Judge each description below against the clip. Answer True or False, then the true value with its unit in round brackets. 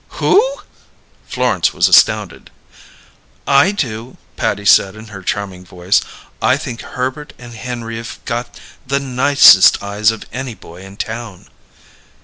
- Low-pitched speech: True (115 Hz)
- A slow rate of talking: True (130 wpm)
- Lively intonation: False (4.2 semitones)